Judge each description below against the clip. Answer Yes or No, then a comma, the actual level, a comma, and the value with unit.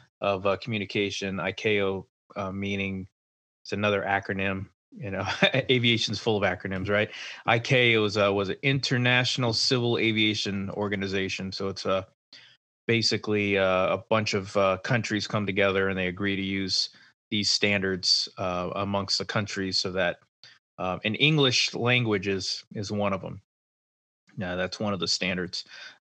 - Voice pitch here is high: No, low, 100 Hz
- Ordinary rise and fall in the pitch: No, narrow, 2.3 semitones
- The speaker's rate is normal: Yes, average, 150 wpm